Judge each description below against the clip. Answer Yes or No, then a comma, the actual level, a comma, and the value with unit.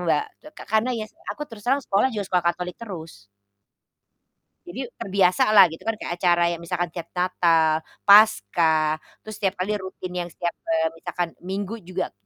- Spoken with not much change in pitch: No, average, 3.4 semitones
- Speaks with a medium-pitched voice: Yes, medium, 180 Hz